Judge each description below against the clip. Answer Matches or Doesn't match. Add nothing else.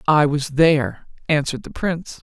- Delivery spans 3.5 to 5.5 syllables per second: Matches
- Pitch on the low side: Doesn't match